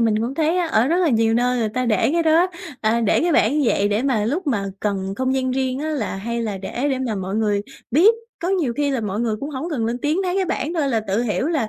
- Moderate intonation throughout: No, wide, 5.7 semitones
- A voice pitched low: No, very high, 250 Hz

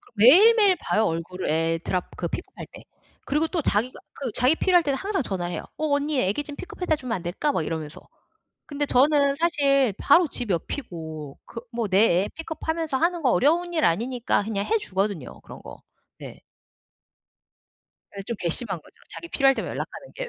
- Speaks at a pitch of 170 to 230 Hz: No, very high, 260 Hz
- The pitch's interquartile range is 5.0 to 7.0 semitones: No, wide, 8.7 semitones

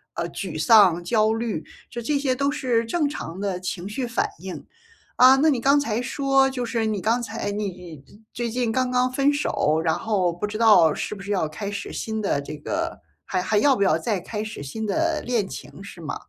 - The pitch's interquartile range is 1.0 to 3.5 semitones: No, average, 5.0 semitones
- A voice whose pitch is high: Yes, high, 220 Hz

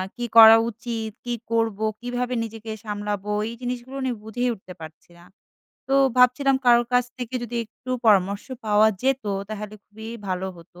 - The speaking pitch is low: No, high, 225 Hz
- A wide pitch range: No, average, 2.9 semitones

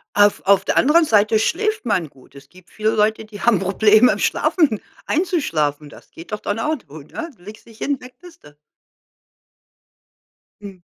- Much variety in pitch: Yes, wide, 6.7 semitones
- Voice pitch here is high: Yes, high, 215 Hz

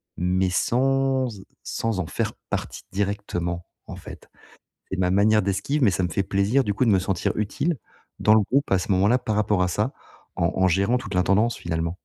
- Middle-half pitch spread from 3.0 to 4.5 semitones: Yes, average, 3.6 semitones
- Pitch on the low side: Yes, low, 100 Hz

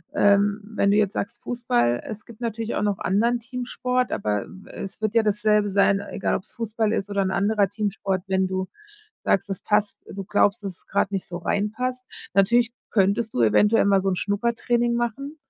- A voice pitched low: No, high, 205 Hz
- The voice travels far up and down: No, average, 2.8 semitones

